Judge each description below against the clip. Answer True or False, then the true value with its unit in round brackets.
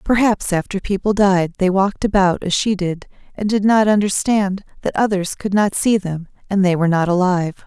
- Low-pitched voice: False (195 Hz)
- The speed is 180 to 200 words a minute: True (195 wpm)